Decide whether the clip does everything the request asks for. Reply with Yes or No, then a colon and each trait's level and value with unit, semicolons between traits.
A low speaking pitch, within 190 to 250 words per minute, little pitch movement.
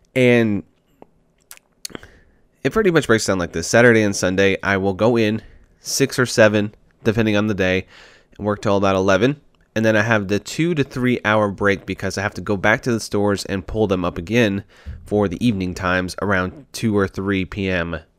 No: low, 100 Hz; average, 200 wpm; average, 3.0 semitones